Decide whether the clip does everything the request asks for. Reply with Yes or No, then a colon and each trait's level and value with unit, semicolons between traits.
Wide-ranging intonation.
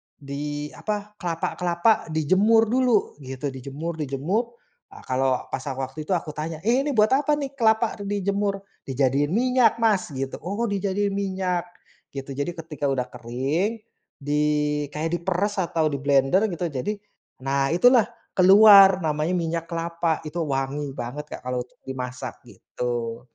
Yes: wide, 6.5 semitones